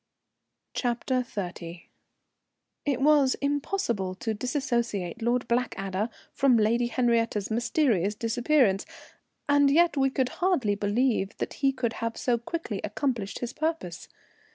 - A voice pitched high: Yes, high, 240 Hz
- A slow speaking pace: Yes, slow, 120 wpm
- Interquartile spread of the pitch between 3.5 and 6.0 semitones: Yes, average, 4.5 semitones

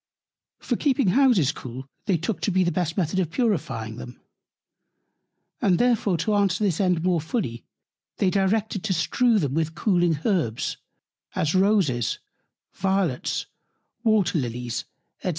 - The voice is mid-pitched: Yes, medium, 180 Hz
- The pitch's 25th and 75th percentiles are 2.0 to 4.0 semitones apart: No, average, 4.7 semitones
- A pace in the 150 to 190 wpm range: No, average, 140 wpm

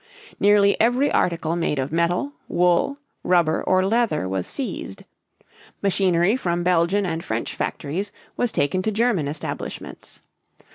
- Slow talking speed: Yes, slow, 130 wpm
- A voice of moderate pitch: Yes, medium, 180 Hz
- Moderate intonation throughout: Yes, average, 3.7 semitones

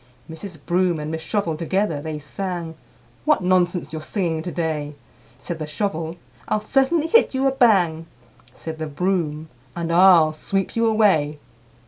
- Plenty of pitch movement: No, average, 3.8 semitones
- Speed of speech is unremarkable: Yes, average, 160 wpm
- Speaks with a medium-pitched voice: Yes, medium, 170 Hz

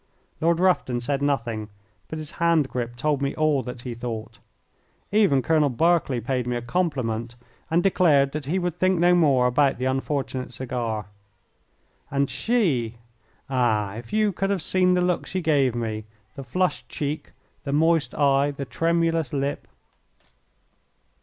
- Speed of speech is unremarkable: Yes, average, 155 wpm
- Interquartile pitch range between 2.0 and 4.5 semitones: No, average, 5.3 semitones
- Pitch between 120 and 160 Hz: Yes, medium, 140 Hz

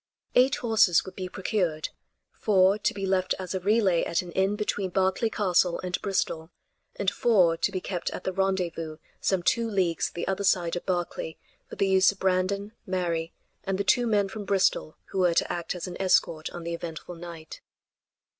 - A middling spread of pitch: No, narrow, 2.3 semitones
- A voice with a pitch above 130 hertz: Yes, medium, 185 Hz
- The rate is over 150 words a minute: Yes, average, 190 wpm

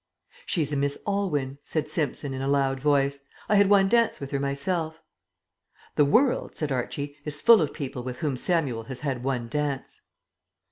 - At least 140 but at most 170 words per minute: No, average, 180 wpm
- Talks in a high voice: No, medium, 145 Hz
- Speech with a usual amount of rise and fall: Yes, average, 3.0 semitones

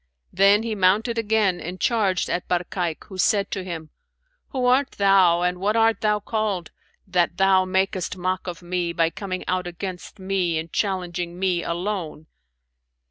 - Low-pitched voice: No, medium, 185 Hz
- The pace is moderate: Yes, average, 160 wpm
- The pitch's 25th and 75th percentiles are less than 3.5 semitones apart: Yes, narrow, 2.4 semitones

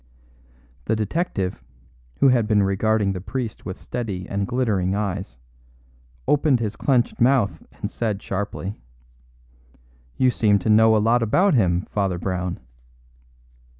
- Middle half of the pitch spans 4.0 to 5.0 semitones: No, average, 3.6 semitones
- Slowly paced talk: Yes, slow, 130 wpm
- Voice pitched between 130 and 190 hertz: No, low, 105 Hz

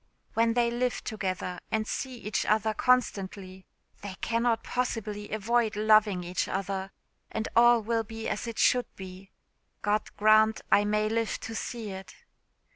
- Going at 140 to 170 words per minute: Yes, average, 150 wpm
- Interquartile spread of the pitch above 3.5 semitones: No, narrow, 2.5 semitones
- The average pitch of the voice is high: Yes, high, 215 Hz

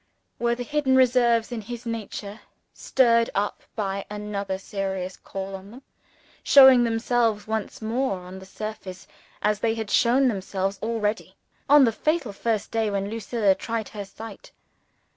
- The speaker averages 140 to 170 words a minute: Yes, average, 150 wpm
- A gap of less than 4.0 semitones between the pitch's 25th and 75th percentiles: Yes, average, 3.0 semitones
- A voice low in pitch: No, high, 220 Hz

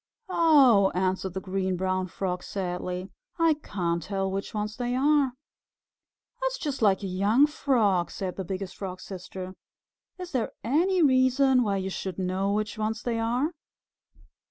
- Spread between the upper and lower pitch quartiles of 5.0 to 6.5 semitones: Yes, wide, 5.6 semitones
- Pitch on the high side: Yes, high, 200 Hz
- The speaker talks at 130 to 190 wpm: Yes, average, 155 wpm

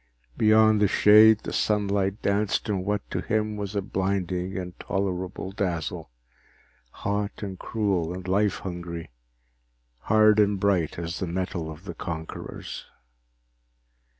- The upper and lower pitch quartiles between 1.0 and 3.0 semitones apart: Yes, narrow, 2.5 semitones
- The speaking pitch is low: Yes, very low, 95 Hz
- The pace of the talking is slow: Yes, slow, 125 wpm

